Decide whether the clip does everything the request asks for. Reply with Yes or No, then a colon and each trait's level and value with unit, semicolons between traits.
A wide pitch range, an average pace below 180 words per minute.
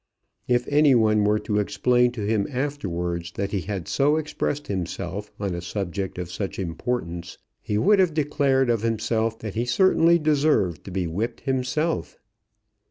Yes: wide, 6.2 semitones; average, 165 wpm